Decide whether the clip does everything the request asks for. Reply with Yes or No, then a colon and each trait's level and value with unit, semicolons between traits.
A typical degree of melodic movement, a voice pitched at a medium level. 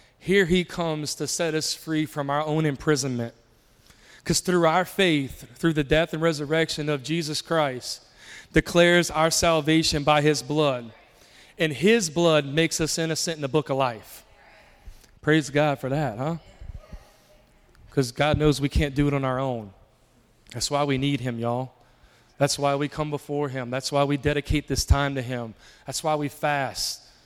Yes: average, 3.0 semitones; medium, 150 Hz